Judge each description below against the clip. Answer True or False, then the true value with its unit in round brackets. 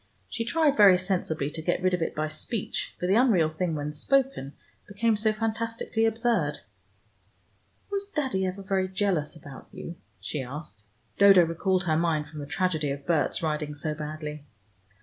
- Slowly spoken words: False (170 wpm)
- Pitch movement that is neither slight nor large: False (5.7 semitones)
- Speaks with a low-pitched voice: False (180 Hz)